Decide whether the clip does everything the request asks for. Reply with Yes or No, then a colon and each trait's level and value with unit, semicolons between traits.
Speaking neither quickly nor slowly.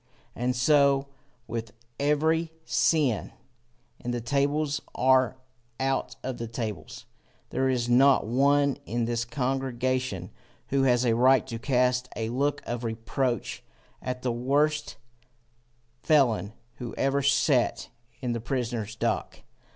No: slow, 125 wpm